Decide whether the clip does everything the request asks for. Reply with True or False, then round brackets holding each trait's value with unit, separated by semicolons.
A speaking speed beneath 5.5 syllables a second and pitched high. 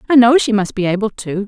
False (6.2 syllables/s; 215 Hz)